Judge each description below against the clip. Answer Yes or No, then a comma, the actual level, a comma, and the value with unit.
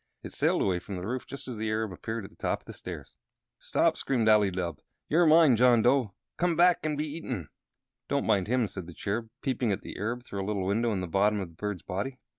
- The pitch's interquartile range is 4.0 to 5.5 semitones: Yes, average, 4.8 semitones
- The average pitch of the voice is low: Yes, low, 110 Hz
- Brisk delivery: Yes, fast, 245 wpm